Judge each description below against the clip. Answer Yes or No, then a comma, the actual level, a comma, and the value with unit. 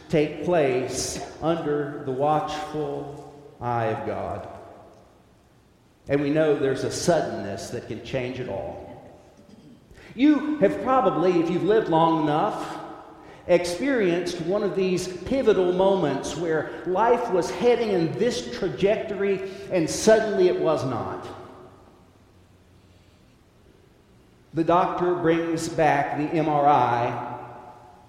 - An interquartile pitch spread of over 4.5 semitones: Yes, wide, 5.4 semitones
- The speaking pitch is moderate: Yes, medium, 160 Hz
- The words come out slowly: Yes, slow, 110 wpm